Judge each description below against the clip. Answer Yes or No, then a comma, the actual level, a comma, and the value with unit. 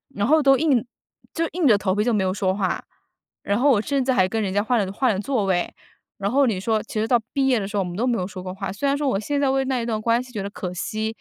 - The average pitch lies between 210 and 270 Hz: Yes, high, 220 Hz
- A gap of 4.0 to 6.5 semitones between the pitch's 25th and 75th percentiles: Yes, average, 5.1 semitones